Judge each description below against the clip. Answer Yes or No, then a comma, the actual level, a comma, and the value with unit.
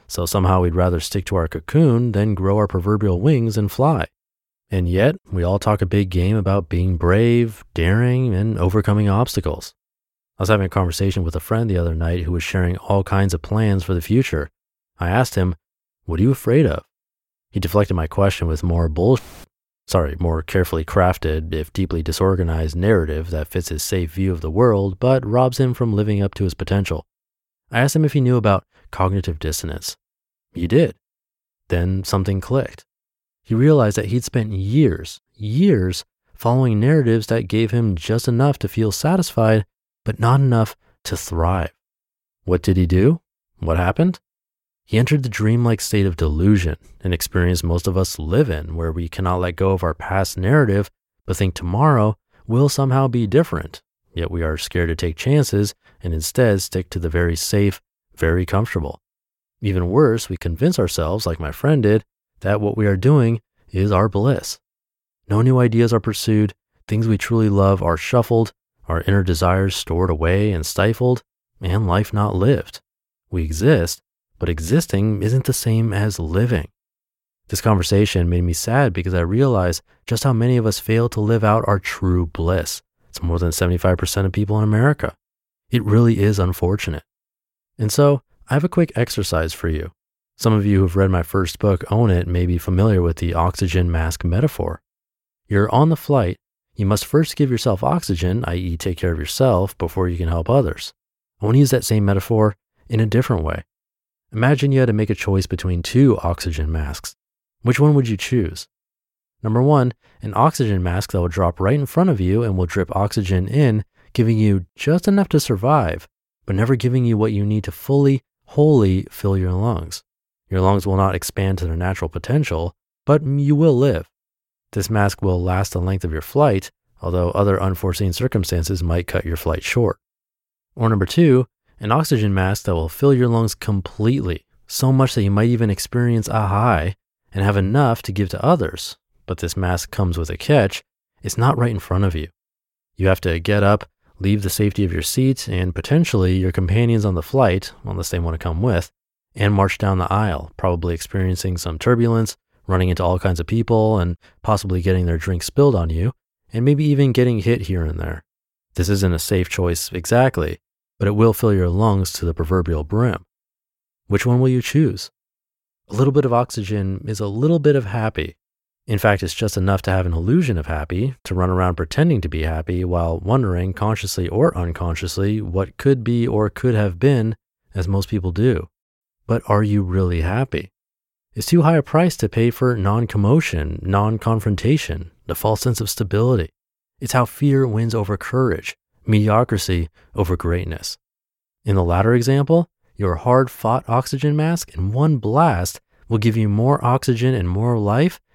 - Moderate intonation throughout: Yes, average, 4.8 semitones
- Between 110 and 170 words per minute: No, average, 185 wpm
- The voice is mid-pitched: No, low, 100 Hz